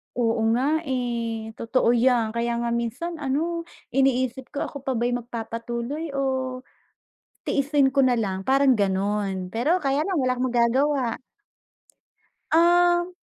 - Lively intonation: No, average, 3.4 semitones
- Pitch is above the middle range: Yes, very high, 250 Hz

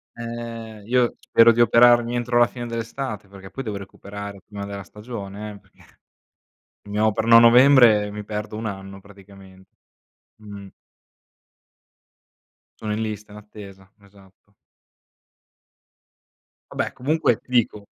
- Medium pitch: No, low, 105 Hz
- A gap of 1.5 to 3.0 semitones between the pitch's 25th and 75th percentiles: Yes, average, 2.7 semitones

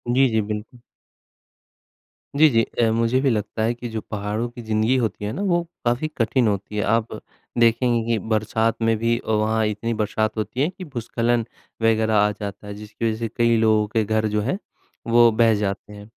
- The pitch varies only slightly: Yes, narrow, 1.8 semitones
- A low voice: Yes, low, 110 Hz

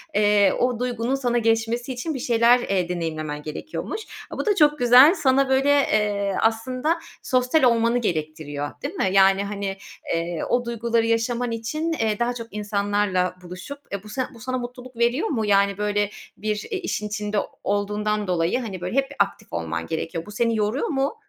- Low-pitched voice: No, high, 225 Hz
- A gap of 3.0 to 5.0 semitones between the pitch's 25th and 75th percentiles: Yes, average, 3.9 semitones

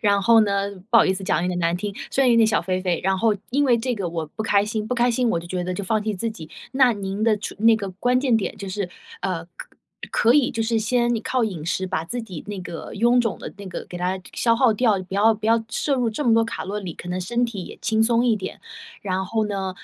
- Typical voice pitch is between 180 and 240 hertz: Yes, high, 210 Hz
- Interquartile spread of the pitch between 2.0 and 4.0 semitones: Yes, average, 3.6 semitones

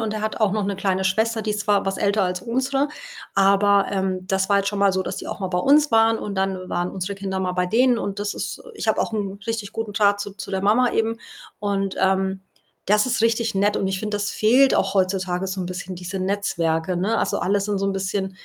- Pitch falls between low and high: No, high, 200 Hz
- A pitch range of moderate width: No, narrow, 2.2 semitones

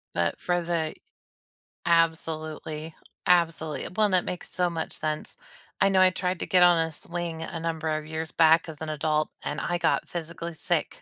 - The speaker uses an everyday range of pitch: No, narrow, 1.8 semitones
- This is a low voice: No, medium, 165 Hz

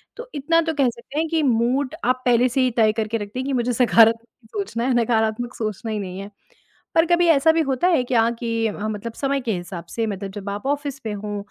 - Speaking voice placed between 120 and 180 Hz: No, high, 235 Hz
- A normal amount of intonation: Yes, average, 4.2 semitones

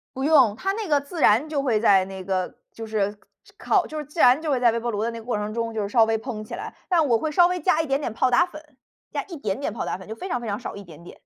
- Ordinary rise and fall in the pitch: No, wide, 6.2 semitones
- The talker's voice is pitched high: Yes, high, 240 Hz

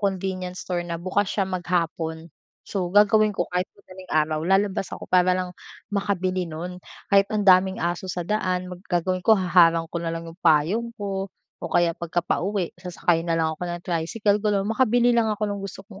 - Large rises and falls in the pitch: No, narrow, 2.6 semitones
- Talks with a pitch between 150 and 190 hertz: Yes, medium, 185 Hz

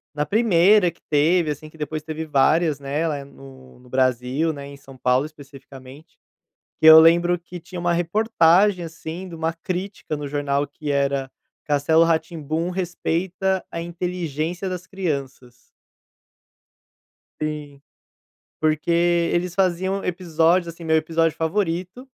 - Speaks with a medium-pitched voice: Yes, medium, 160 Hz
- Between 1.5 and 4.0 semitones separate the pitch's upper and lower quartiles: Yes, average, 3.4 semitones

